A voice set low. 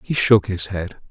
Yes: very low, 95 Hz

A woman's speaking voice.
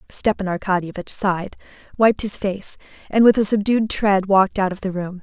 Yes: female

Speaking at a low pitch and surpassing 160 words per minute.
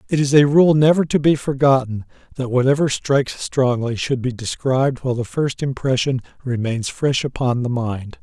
Yes: low, 130 Hz; average, 175 wpm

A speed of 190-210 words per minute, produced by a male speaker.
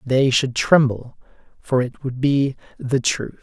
No: average, 160 wpm; male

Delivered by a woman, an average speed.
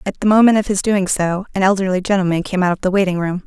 No: female; fast, 275 wpm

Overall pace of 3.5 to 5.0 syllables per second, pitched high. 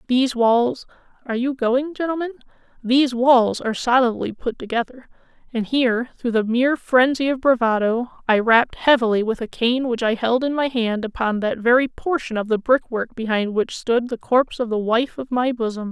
No: 5.3 syllables/s; high, 245 Hz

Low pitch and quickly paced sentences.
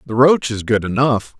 Yes: low, 125 Hz; fast, 215 wpm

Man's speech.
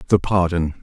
Yes: male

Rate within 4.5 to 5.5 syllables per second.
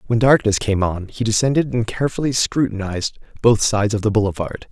No: 6.0 syllables/s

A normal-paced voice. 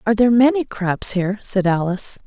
Yes: average, 185 wpm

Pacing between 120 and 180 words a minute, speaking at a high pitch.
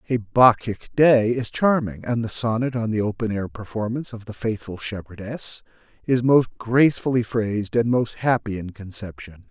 No: average, 165 wpm; low, 115 Hz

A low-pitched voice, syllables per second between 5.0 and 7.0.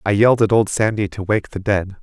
Yes: low, 105 Hz; 5.8 syllables/s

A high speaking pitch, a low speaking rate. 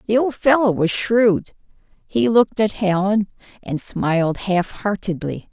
Yes: high, 200 Hz; slow, 130 wpm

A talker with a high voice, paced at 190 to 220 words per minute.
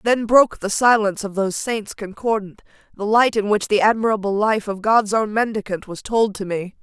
Yes: high, 210 Hz; average, 200 wpm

